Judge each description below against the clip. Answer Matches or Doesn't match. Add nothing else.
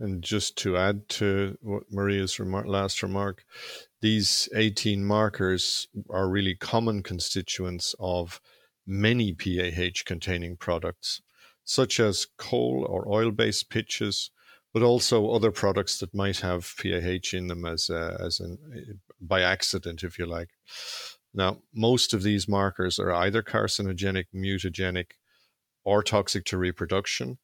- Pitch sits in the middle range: Doesn't match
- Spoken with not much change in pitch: Matches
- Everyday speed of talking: Doesn't match